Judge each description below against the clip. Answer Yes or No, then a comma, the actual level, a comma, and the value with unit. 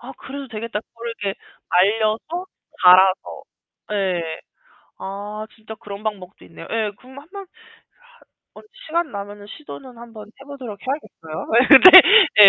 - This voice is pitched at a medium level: No, high, 215 Hz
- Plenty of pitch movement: No, average, 4.5 semitones